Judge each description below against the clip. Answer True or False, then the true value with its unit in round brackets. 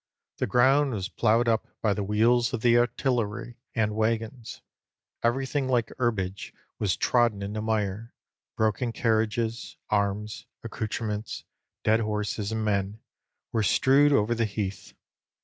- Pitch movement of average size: False (2.3 semitones)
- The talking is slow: True (130 wpm)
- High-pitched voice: False (110 Hz)